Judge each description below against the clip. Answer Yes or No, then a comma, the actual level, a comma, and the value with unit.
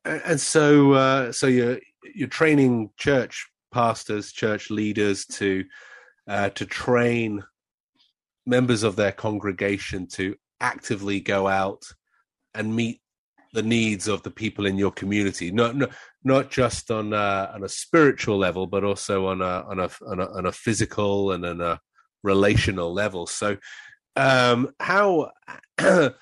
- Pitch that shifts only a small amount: No, average, 3.4 semitones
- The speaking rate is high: No, average, 140 wpm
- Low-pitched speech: Yes, low, 105 Hz